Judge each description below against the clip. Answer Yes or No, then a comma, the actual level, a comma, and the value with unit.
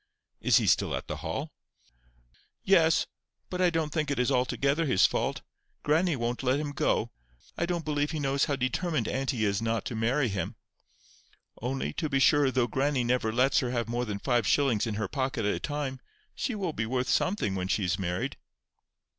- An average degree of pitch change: Yes, average, 4.4 semitones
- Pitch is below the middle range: Yes, low, 130 Hz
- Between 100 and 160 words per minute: No, average, 195 wpm